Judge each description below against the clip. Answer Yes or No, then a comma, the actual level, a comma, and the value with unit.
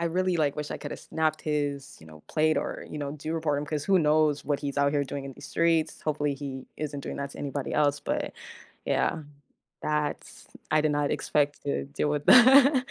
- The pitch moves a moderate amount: No, narrow, 1.7 semitones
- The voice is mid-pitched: Yes, medium, 150 Hz